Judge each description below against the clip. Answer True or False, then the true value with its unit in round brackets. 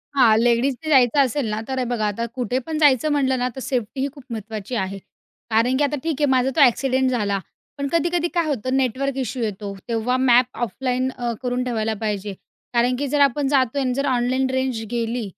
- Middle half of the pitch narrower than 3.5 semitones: True (2.7 semitones)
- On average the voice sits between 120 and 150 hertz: False (255 Hz)